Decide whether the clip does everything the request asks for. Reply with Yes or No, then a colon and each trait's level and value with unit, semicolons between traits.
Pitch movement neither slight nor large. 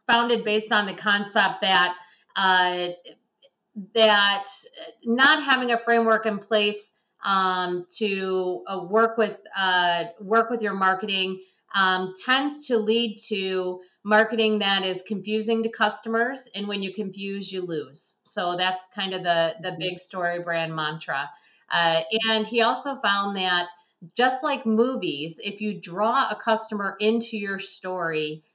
Yes: average, 3.3 semitones